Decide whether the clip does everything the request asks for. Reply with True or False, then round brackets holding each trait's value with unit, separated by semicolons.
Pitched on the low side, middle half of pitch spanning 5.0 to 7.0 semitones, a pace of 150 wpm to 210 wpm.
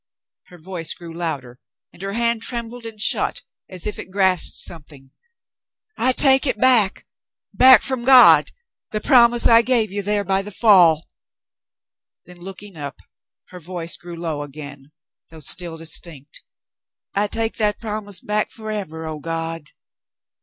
False (190 Hz; 5.4 semitones; 155 wpm)